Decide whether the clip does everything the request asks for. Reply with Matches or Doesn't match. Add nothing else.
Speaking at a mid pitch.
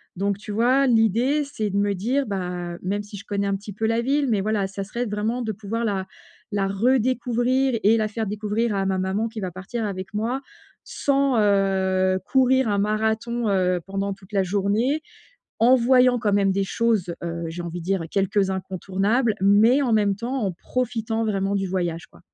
Doesn't match